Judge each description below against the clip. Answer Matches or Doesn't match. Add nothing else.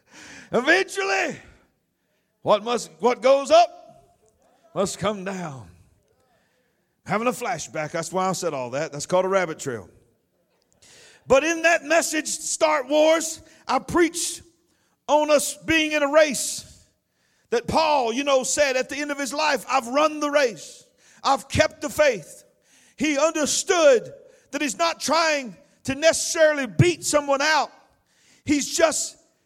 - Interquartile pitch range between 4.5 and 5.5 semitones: Matches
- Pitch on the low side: Doesn't match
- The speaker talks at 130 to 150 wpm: Matches